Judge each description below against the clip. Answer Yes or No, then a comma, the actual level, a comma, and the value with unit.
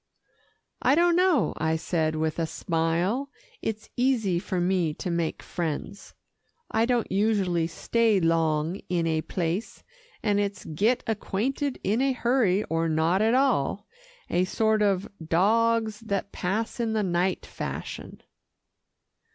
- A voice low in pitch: No, high, 195 Hz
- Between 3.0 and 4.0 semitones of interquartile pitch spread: No, average, 5.3 semitones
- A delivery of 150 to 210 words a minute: No, slow, 135 wpm